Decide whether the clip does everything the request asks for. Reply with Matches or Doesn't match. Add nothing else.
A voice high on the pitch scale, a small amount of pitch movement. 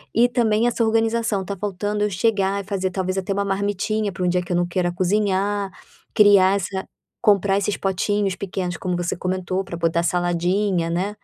Matches